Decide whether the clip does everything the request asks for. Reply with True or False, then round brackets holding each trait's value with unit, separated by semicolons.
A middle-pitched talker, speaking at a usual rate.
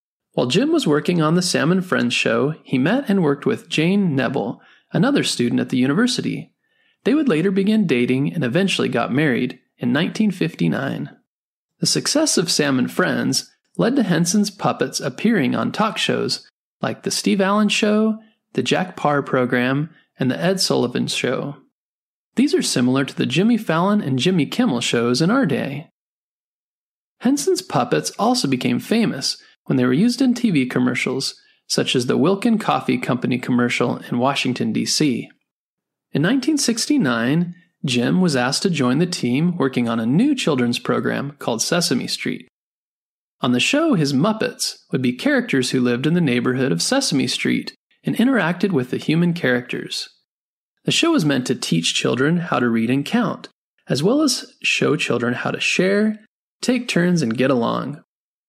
True (175 Hz; 165 wpm)